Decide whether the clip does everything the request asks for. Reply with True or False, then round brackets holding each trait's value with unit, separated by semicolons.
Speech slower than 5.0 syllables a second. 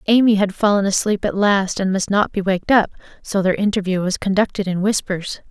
False (5.6 syllables/s)